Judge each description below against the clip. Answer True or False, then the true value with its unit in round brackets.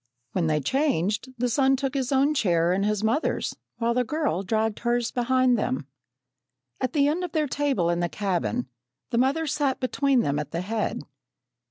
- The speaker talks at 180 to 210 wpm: True (185 wpm)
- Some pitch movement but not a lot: False (6.7 semitones)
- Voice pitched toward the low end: False (240 Hz)